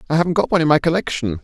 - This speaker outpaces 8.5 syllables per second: Yes, 8.8 syllables/s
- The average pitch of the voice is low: No, medium, 155 Hz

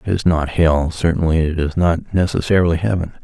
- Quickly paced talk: No, average, 185 wpm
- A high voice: No, very low, 85 Hz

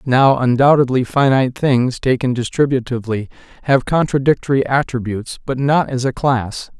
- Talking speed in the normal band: No, slow, 125 wpm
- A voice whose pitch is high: No, low, 130 Hz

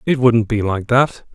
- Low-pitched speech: Yes, low, 115 Hz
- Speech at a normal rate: No, fast, 225 wpm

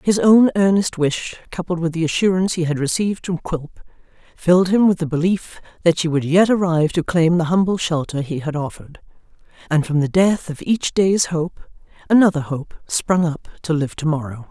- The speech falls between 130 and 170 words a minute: No, average, 195 wpm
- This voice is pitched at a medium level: Yes, medium, 170 Hz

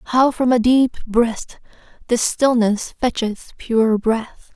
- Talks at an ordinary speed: No, slow, 130 wpm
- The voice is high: Yes, high, 235 Hz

